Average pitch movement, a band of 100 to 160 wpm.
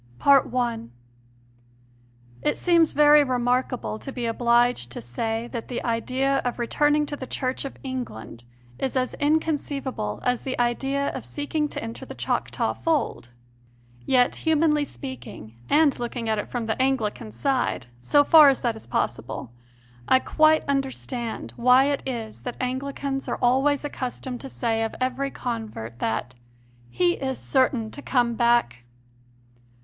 Yes: average, 3.3 semitones; average, 145 wpm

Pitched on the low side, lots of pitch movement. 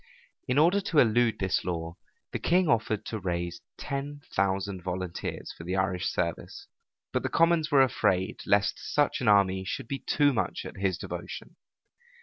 Yes: low, 100 Hz; wide, 7.0 semitones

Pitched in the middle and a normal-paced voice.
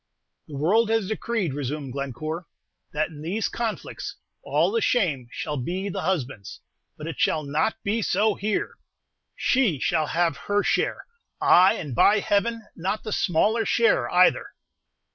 Yes: medium, 180 Hz; average, 150 wpm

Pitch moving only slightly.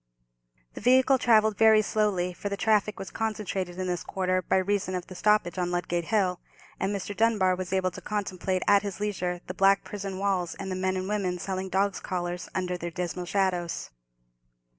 Yes: narrow, 2.2 semitones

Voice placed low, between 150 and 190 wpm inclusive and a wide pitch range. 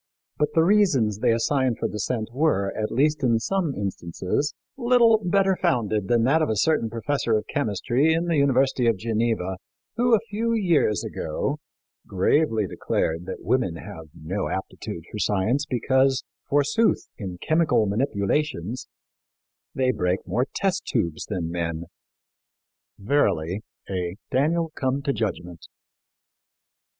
No: low, 120 Hz; slow, 135 wpm; wide, 7.2 semitones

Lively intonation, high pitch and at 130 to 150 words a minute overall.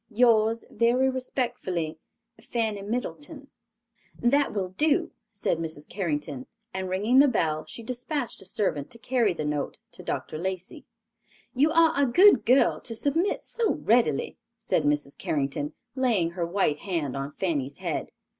Yes: wide, 7.9 semitones; high, 210 Hz; average, 145 wpm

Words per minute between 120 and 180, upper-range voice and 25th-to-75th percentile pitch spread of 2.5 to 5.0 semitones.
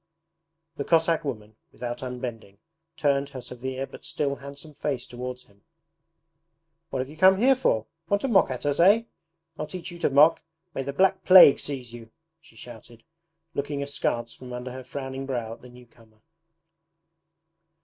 No: average, 170 wpm; low, 135 Hz; average, 3.8 semitones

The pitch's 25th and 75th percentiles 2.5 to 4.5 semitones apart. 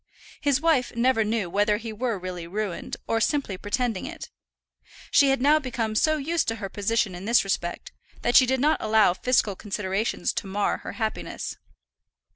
Yes: average, 4.2 semitones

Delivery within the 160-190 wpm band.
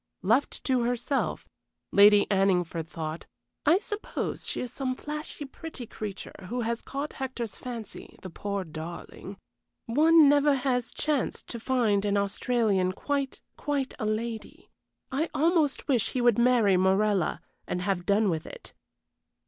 No: average, 140 wpm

